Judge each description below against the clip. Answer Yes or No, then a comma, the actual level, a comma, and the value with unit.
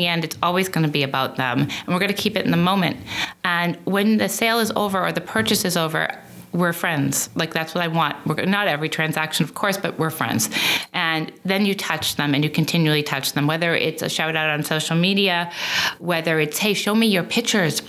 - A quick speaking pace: Yes, fast, 230 wpm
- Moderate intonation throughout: Yes, average, 3.6 semitones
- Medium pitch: Yes, medium, 170 Hz